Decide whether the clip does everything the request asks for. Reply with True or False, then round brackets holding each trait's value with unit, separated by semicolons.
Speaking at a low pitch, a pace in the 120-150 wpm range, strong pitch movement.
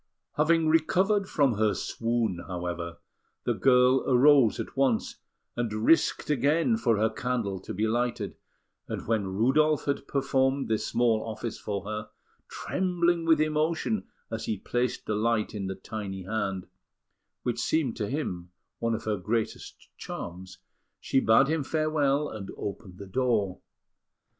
True (120 Hz; 145 wpm; 5.7 semitones)